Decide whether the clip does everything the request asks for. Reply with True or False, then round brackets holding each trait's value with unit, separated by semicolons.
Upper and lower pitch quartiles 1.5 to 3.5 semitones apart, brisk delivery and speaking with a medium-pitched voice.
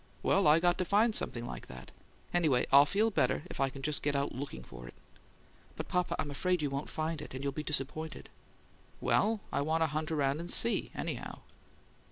False (4.1 semitones; 210 wpm; 150 Hz)